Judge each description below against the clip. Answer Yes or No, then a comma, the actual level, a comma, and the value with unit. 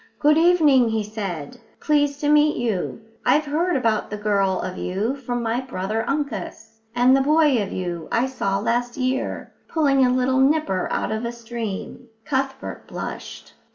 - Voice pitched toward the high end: Yes, high, 245 Hz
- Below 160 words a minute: No, average, 165 wpm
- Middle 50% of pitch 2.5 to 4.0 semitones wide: No, average, 4.5 semitones